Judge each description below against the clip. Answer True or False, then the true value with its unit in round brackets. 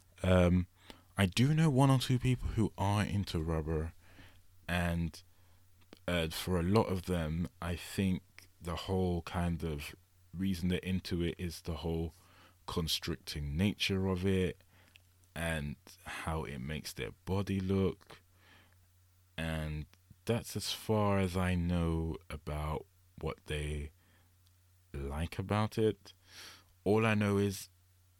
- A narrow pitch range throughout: True (2.2 semitones)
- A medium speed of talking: False (130 wpm)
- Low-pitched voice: True (90 Hz)